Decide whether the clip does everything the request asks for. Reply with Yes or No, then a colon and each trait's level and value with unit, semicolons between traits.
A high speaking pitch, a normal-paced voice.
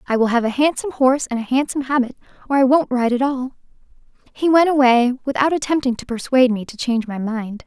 No: very high, 255 Hz; fast, 220 wpm